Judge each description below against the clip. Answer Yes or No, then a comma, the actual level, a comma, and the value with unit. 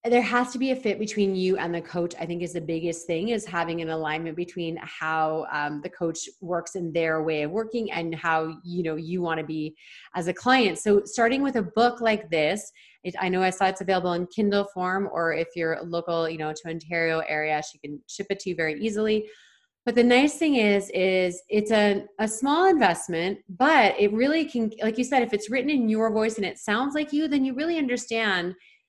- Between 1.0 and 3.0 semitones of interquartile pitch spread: No, average, 5.1 semitones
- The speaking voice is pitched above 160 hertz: Yes, medium, 185 Hz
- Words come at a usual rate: No, fast, 225 wpm